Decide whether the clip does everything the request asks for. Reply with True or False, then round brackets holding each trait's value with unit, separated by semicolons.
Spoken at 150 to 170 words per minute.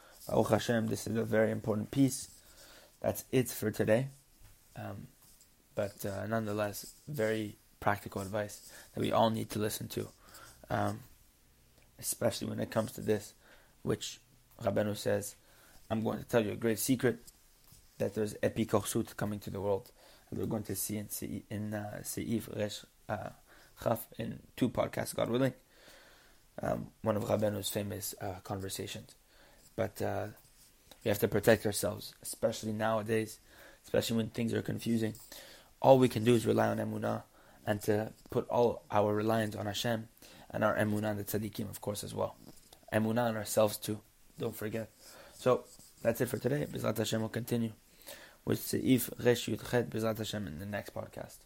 True (165 wpm)